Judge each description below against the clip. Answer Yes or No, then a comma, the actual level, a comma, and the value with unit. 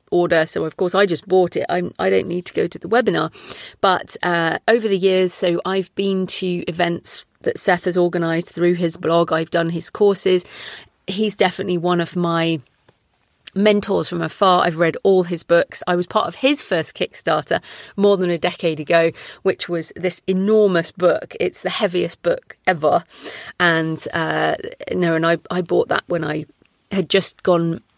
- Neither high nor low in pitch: Yes, medium, 175 Hz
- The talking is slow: No, average, 185 wpm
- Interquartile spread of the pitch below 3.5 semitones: Yes, narrow, 2.4 semitones